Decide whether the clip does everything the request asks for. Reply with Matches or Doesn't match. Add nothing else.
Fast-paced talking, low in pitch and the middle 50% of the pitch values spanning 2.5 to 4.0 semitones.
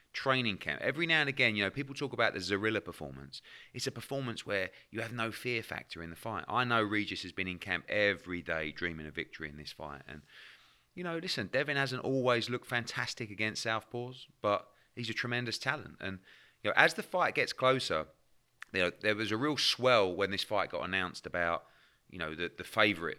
Doesn't match